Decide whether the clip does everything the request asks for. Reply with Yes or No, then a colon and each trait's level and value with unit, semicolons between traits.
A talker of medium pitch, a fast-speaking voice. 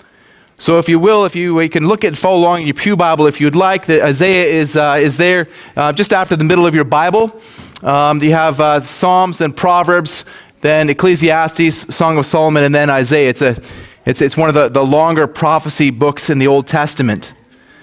Yes: medium, 155 Hz; fast, 210 wpm